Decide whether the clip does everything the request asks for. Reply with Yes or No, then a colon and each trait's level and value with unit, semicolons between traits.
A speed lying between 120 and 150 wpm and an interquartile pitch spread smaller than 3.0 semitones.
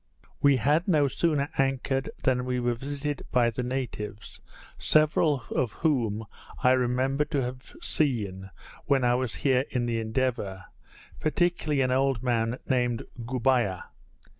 Yes: average, 140 wpm; narrow, 2.6 semitones